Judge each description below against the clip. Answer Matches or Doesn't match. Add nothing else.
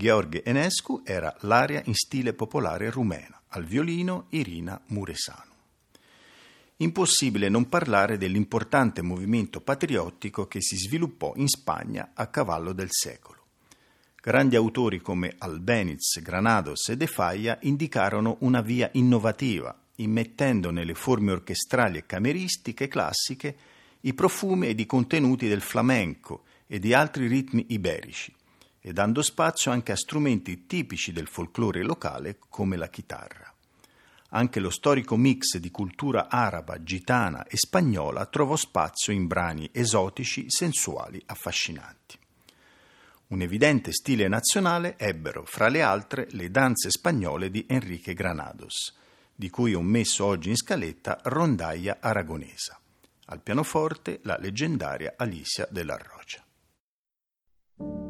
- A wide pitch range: Matches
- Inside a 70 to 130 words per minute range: Matches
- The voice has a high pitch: Doesn't match